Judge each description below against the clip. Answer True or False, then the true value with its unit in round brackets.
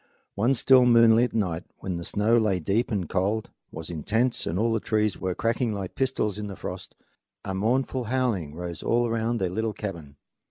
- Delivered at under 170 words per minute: False (195 wpm)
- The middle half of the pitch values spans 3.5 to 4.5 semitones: True (3.9 semitones)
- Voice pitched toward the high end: False (105 Hz)